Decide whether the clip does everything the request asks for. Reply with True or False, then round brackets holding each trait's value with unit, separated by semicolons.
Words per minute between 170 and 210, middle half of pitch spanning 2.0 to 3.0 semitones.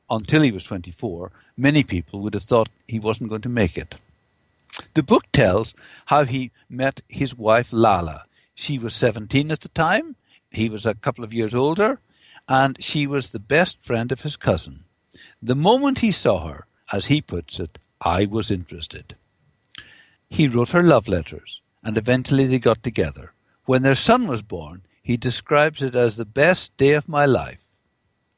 False (175 wpm; 5.0 semitones)